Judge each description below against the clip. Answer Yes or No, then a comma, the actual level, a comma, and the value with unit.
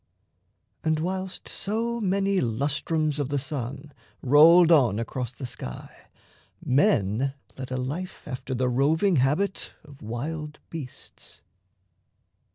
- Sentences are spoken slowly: Yes, slow, 115 wpm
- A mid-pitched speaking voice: Yes, medium, 145 Hz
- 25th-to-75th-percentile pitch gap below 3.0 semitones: No, average, 4.8 semitones